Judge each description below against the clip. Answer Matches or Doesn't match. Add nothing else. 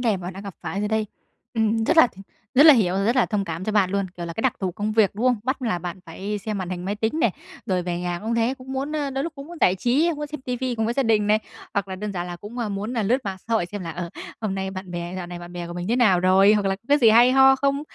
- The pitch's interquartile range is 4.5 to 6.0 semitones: Matches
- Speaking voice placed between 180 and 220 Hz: Matches